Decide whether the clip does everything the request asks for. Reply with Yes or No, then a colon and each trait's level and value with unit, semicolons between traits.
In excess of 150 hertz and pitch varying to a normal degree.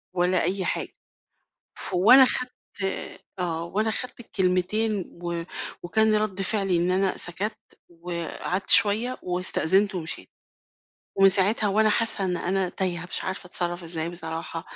Yes: medium, 185 Hz; average, 3.1 semitones